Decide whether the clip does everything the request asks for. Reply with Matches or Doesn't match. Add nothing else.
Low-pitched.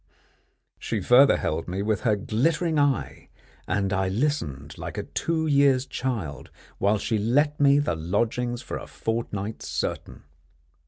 Matches